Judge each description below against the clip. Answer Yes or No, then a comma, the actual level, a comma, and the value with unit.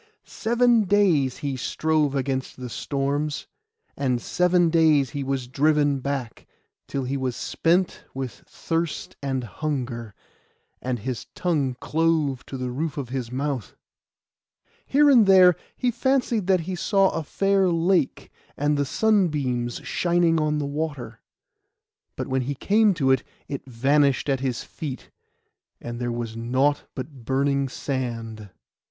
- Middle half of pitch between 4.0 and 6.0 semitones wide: Yes, average, 4.4 semitones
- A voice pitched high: No, medium, 140 Hz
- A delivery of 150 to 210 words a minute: No, average, 140 wpm